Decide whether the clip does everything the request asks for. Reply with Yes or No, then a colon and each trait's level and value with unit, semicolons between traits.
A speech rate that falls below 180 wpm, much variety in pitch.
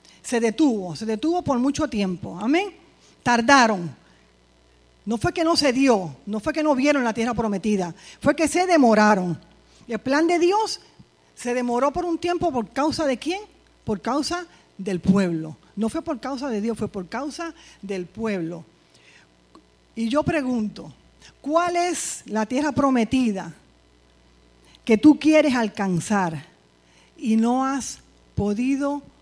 Yes: average, 150 wpm; wide, 8.0 semitones